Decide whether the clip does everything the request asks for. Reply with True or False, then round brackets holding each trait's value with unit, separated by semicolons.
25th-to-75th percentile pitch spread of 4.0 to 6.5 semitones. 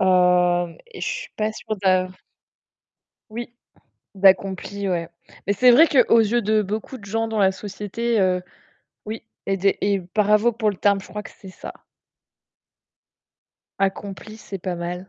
False (2.7 semitones)